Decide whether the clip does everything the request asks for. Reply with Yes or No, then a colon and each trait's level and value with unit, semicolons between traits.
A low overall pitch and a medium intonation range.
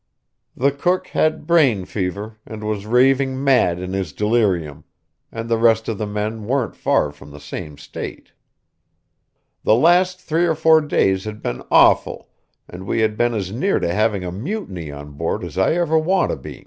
No: low, 110 Hz; wide, 6.8 semitones